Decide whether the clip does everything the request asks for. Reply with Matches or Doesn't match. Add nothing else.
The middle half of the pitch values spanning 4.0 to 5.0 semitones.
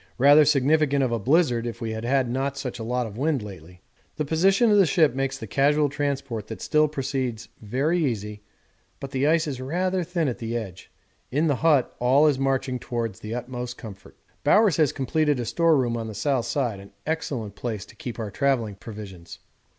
Matches